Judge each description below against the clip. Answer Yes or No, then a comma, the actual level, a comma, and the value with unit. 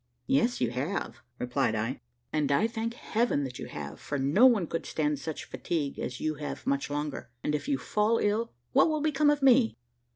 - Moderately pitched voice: Yes, medium, 160 Hz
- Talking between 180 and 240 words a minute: Yes, average, 200 wpm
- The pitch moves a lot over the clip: Yes, wide, 8.9 semitones